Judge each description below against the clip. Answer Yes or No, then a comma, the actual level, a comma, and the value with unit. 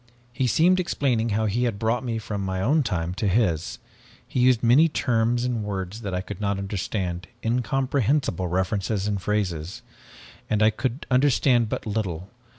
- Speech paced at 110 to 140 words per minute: No, average, 165 wpm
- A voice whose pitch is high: No, low, 110 Hz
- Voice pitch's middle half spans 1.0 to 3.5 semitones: No, average, 4.3 semitones